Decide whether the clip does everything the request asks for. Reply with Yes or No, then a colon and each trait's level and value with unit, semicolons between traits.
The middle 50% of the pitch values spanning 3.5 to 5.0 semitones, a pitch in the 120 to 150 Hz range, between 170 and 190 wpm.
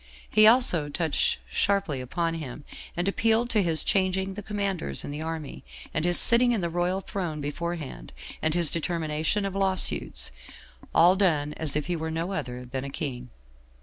No: average, 4.2 semitones; medium, 170 Hz; average, 180 wpm